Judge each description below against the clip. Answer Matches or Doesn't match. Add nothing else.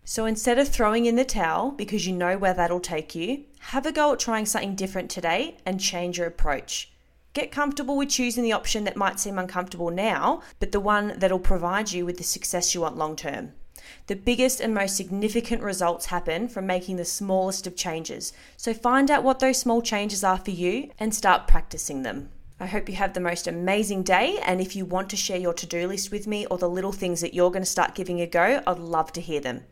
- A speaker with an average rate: Doesn't match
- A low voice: Doesn't match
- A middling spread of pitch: Matches